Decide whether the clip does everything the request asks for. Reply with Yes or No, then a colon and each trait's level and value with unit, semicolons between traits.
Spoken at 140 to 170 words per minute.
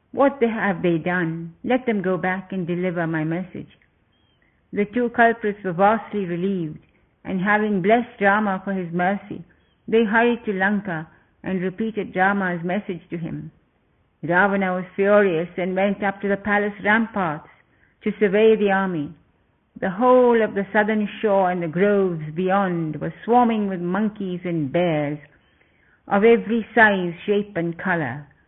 Yes: average, 150 wpm